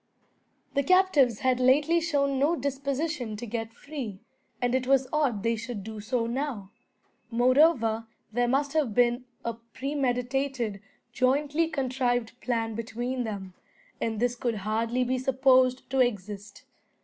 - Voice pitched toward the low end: No, very high, 250 Hz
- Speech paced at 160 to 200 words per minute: No, slow, 135 wpm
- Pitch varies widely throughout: No, average, 3.2 semitones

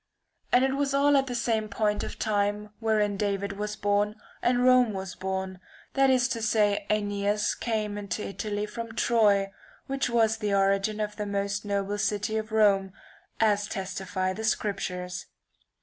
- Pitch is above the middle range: Yes, high, 210 Hz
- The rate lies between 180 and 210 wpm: No, average, 165 wpm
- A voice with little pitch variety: Yes, narrow, 1.8 semitones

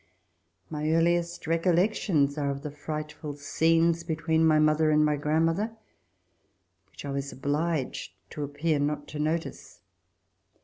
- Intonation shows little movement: Yes, narrow, 2.1 semitones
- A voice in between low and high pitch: Yes, medium, 155 Hz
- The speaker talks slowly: Yes, slow, 130 wpm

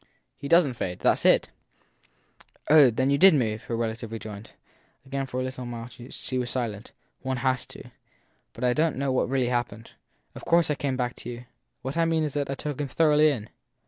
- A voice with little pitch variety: No, average, 3.2 semitones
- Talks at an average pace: No, fast, 220 wpm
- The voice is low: Yes, low, 130 Hz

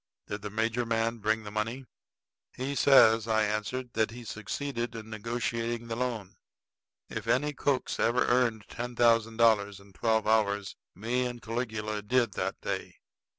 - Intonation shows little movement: Yes, narrow, 2.1 semitones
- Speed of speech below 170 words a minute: Yes, average, 155 wpm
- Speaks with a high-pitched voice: No, low, 115 Hz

